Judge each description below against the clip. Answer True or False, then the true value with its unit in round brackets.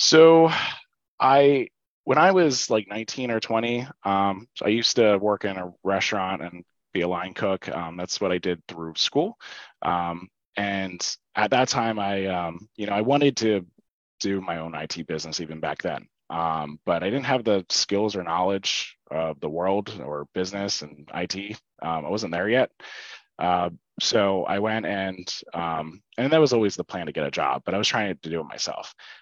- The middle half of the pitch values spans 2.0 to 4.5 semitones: True (3.7 semitones)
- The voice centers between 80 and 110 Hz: True (95 Hz)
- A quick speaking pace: False (195 wpm)